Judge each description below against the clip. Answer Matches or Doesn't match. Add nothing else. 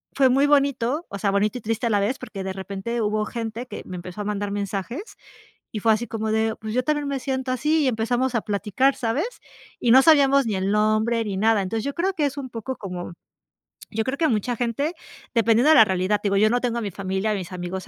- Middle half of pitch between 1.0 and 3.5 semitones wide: Doesn't match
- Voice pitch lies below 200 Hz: Doesn't match